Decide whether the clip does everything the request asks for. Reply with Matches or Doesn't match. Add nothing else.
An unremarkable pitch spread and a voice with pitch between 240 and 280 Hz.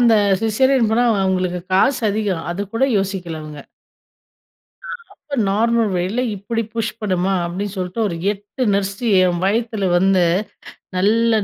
Doesn't match